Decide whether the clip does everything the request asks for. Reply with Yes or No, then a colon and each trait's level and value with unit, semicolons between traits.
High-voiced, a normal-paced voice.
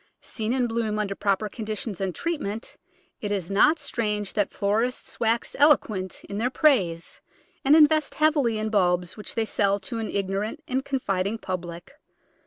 Yes: high, 215 Hz; average, 165 wpm